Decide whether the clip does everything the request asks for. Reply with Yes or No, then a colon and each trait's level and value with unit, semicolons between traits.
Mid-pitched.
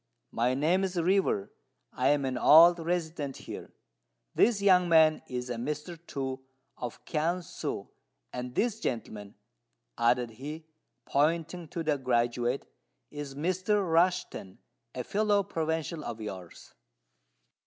Yes: medium, 150 Hz